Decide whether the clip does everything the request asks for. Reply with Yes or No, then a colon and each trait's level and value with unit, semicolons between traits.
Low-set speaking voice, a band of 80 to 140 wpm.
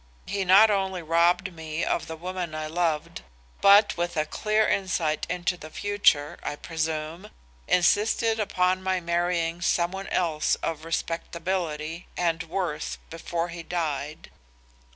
No: medium, 170 Hz; slow, 135 wpm